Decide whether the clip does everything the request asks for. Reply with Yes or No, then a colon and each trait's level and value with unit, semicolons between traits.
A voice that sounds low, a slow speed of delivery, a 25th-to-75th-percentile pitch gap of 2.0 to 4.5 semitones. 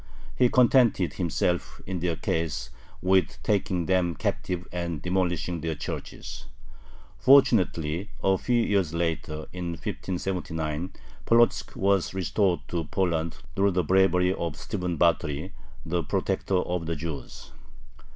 Yes: very low, 90 Hz; slow, 120 wpm; narrow, 2.6 semitones